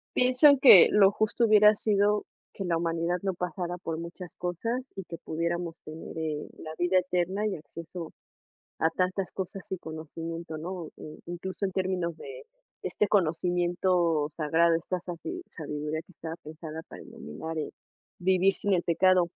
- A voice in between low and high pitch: Yes, medium, 175 Hz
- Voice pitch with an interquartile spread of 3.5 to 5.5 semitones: No, average, 2.7 semitones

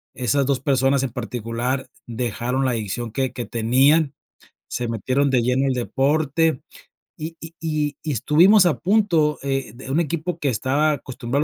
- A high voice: No, low, 135 Hz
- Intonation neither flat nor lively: Yes, average, 3.6 semitones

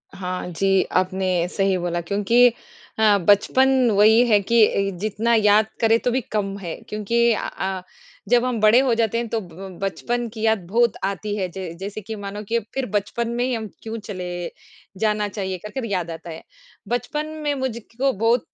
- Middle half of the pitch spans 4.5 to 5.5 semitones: No, average, 3.3 semitones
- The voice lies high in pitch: Yes, high, 210 Hz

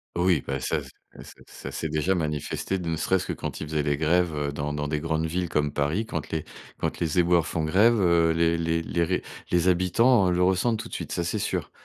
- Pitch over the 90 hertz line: No, very low, 85 Hz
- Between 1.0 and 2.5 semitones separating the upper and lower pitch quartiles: No, average, 2.9 semitones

